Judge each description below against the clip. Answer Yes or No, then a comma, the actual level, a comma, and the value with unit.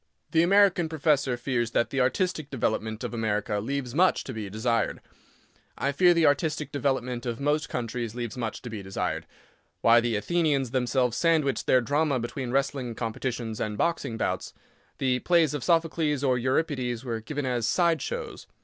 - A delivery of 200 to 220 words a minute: No, average, 165 wpm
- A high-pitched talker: No, low, 130 Hz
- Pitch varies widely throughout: No, average, 4.3 semitones